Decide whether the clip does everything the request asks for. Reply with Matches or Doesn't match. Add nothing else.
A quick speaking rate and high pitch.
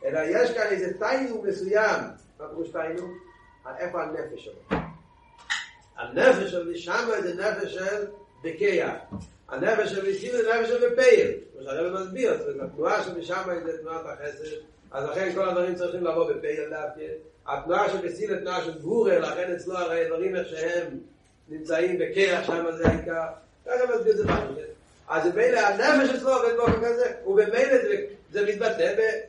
Matches